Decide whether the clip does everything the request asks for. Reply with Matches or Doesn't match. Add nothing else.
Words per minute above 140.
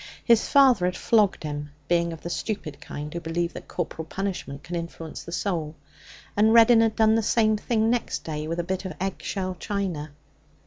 Matches